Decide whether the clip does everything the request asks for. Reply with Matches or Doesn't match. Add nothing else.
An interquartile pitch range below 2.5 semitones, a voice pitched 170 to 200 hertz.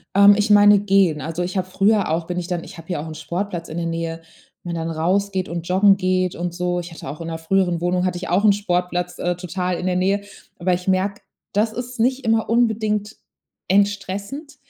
Doesn't match